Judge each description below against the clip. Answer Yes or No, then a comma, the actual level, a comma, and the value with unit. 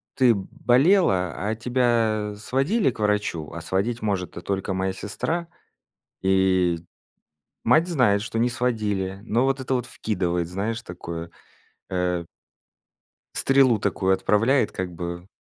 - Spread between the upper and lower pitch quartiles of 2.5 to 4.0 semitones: No, average, 4.7 semitones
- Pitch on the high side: No, low, 105 Hz